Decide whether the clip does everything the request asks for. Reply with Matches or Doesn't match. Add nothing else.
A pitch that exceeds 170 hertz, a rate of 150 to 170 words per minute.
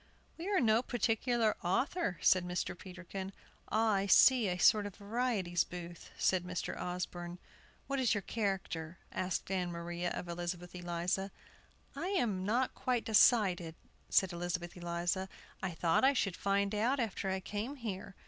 Matches